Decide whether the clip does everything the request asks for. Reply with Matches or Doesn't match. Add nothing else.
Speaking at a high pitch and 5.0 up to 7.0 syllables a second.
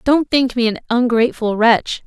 Doesn't match